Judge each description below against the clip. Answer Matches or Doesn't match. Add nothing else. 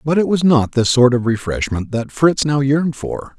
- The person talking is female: Doesn't match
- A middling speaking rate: Doesn't match